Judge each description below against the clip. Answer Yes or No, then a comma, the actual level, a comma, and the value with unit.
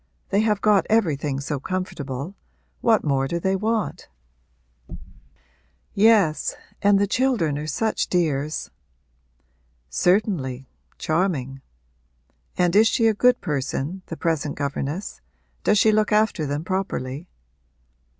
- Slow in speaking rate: Yes, slow, 115 wpm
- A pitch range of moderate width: No, wide, 6.5 semitones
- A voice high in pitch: No, medium, 180 Hz